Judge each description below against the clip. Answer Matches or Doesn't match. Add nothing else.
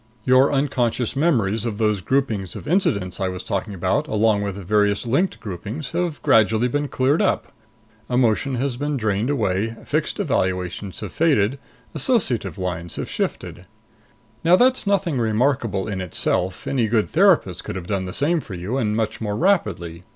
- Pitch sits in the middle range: Doesn't match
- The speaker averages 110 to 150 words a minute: Doesn't match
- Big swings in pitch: Matches